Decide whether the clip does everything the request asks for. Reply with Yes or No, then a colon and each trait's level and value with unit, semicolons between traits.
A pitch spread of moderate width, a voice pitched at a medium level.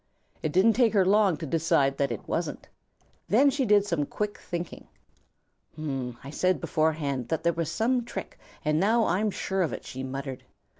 No: wide, 6.7 semitones; medium, 165 Hz